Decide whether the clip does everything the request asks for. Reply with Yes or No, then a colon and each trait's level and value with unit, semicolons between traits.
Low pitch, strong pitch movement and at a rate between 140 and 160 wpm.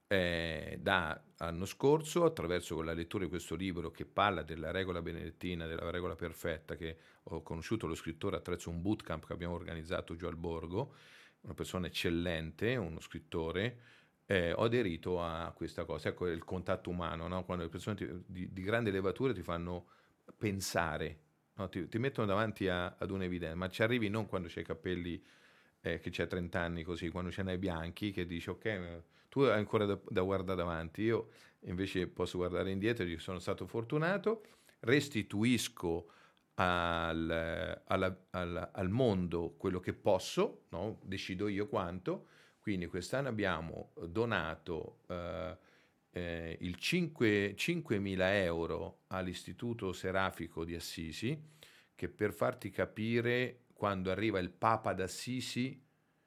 No: very low, 90 Hz; average, 3.6 semitones; average, 150 wpm